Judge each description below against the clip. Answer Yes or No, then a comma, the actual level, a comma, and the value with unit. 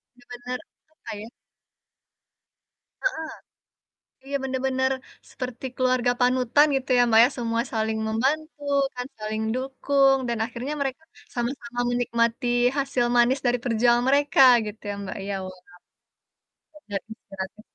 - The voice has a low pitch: No, high, 245 Hz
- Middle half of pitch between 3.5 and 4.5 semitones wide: No, narrow, 2.5 semitones